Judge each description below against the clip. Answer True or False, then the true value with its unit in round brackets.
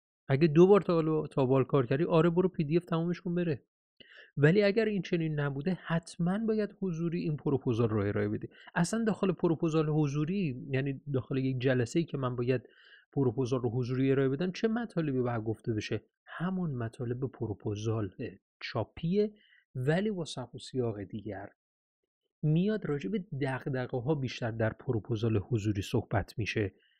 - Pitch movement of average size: False (5.9 semitones)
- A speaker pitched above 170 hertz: False (140 Hz)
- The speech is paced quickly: True (160 wpm)